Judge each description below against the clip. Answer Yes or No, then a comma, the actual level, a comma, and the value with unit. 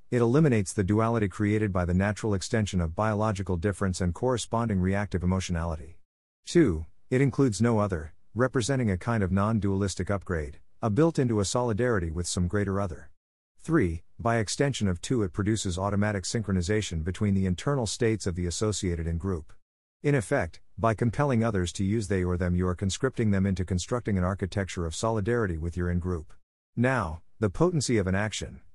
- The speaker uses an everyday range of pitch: Yes, average, 4.1 semitones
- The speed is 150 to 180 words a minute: Yes, average, 175 wpm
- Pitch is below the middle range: Yes, low, 100 Hz